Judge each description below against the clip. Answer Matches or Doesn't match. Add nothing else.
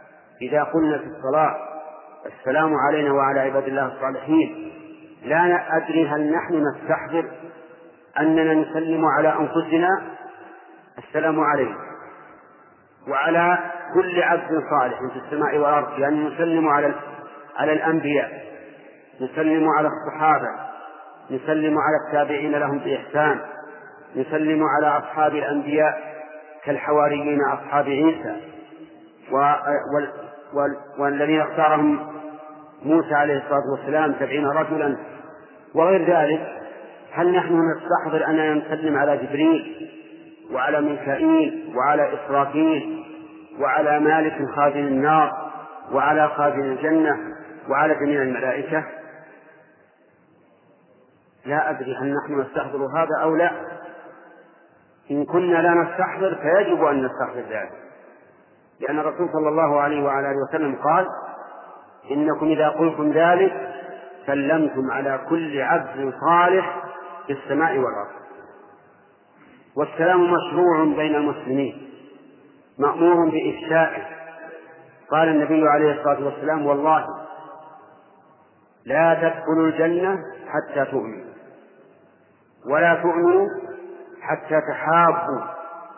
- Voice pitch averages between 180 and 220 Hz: Doesn't match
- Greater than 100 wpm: Doesn't match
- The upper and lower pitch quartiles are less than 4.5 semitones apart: Matches